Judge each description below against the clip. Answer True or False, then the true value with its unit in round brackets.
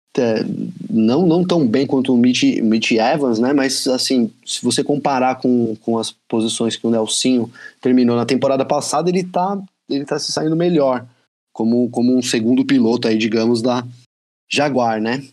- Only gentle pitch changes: False (3.2 semitones)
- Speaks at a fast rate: False (170 wpm)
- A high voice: False (125 Hz)